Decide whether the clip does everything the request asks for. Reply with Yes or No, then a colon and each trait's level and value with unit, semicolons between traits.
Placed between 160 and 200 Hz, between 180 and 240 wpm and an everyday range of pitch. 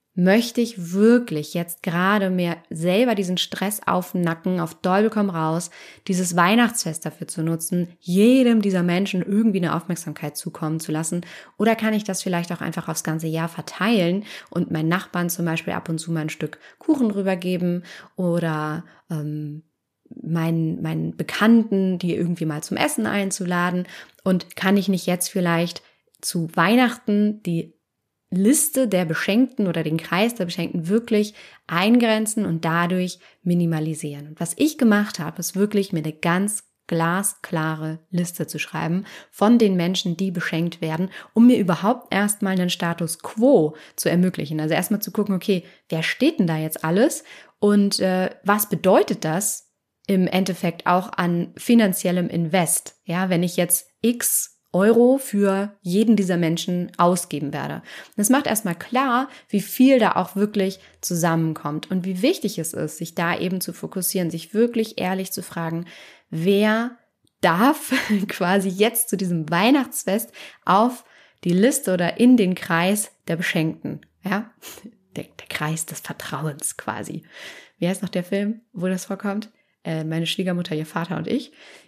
No: medium, 185 Hz; average, 155 wpm; average, 3.6 semitones